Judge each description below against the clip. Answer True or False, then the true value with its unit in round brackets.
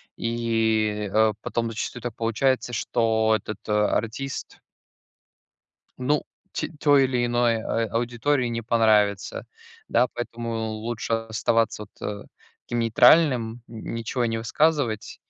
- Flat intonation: True (1.8 semitones)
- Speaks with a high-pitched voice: False (115 Hz)